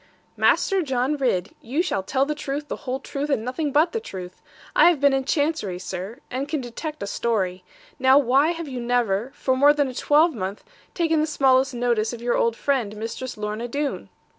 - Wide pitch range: No, average, 4.3 semitones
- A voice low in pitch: No, very high, 260 Hz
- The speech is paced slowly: No, average, 200 wpm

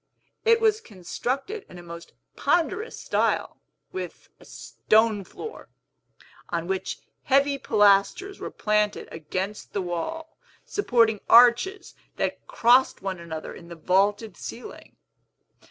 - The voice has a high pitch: Yes, high, 215 Hz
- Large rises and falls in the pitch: Yes, wide, 7.2 semitones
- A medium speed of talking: No, slow, 120 wpm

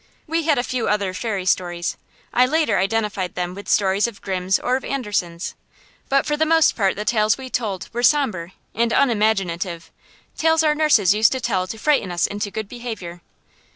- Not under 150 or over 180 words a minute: No, average, 190 wpm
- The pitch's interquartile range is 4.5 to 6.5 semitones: Yes, wide, 5.4 semitones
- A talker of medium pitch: No, high, 215 Hz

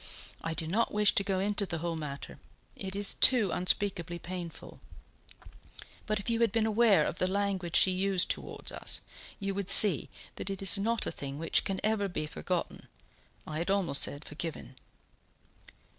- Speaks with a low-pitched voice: No, high, 190 Hz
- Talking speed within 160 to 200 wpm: Yes, average, 175 wpm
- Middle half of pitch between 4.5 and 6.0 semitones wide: No, average, 3.3 semitones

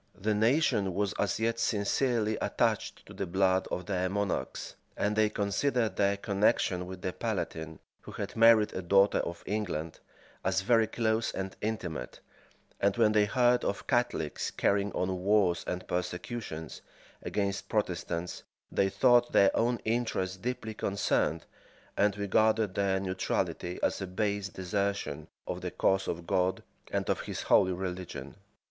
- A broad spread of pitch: No, average, 2.8 semitones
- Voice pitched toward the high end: No, low, 100 Hz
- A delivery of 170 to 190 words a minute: No, average, 150 wpm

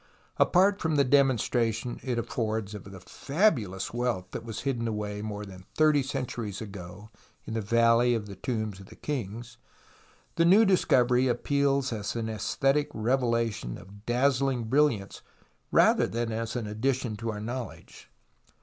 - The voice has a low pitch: Yes, low, 115 Hz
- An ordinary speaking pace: Yes, average, 150 wpm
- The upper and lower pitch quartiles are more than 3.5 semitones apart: Yes, average, 4.0 semitones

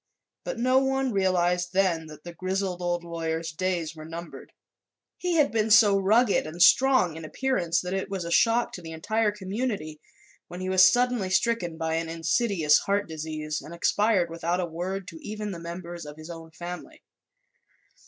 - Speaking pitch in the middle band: Yes, medium, 180 Hz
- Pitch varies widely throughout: No, average, 4.0 semitones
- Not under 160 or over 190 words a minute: Yes, average, 180 wpm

